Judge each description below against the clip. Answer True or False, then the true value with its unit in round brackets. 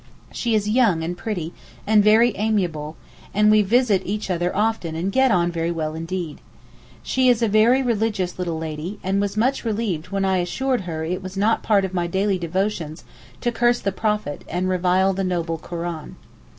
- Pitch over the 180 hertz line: True (190 Hz)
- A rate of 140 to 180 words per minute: False (190 wpm)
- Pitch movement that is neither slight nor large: True (3.9 semitones)